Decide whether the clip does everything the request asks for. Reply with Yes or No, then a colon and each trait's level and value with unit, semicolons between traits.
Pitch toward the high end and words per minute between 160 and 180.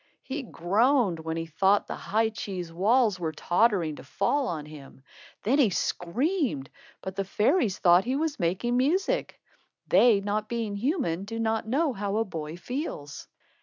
Yes: high, 205 Hz; average, 165 wpm